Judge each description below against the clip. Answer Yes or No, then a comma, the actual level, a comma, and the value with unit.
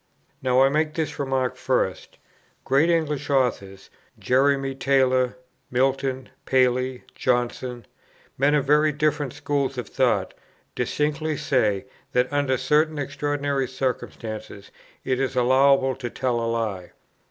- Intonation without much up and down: Yes, narrow, 2.3 semitones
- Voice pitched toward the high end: No, low, 135 Hz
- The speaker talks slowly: Yes, slow, 120 wpm